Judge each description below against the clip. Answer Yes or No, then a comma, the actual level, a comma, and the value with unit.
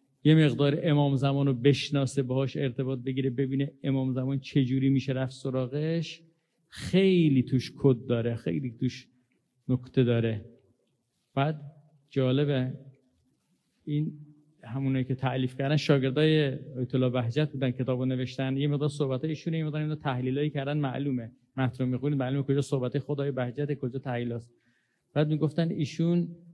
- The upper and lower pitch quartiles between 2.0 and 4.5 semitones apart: Yes, narrow, 2.4 semitones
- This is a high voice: No, low, 135 Hz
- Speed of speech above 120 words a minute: Yes, average, 135 wpm